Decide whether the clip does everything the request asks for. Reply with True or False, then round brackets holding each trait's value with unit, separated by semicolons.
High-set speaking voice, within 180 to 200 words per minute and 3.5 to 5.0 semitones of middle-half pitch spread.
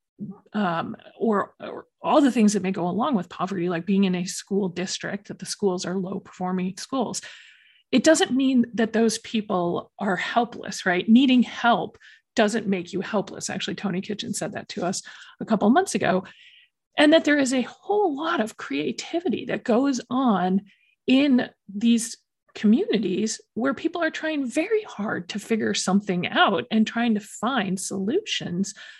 False (220 Hz; 170 wpm; 4.7 semitones)